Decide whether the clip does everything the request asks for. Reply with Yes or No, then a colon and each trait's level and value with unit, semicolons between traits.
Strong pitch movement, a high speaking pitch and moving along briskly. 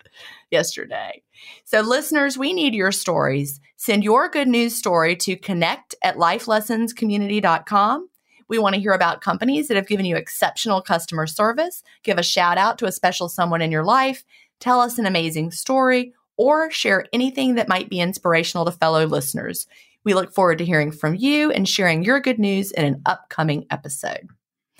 No: wide, 6.5 semitones; high, 200 Hz; average, 170 wpm